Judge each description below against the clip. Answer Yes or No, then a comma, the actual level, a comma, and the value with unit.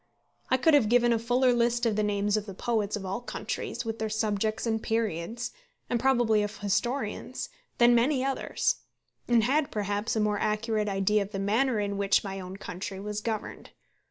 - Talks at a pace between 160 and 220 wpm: Yes, average, 190 wpm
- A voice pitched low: No, high, 220 Hz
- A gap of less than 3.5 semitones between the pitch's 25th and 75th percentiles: Yes, average, 2.7 semitones